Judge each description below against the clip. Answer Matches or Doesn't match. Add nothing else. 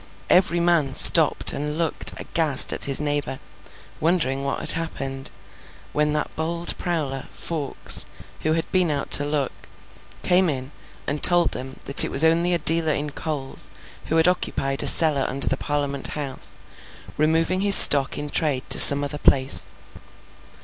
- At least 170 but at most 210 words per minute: Doesn't match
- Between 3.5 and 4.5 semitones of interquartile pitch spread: Doesn't match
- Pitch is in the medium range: Matches